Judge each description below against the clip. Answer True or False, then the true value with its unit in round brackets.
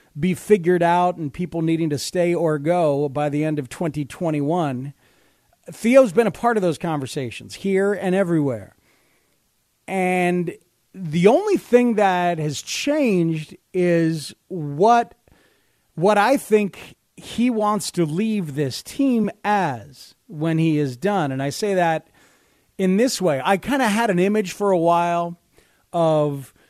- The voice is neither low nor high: True (175 Hz)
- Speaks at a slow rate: False (145 wpm)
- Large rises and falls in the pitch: False (4.7 semitones)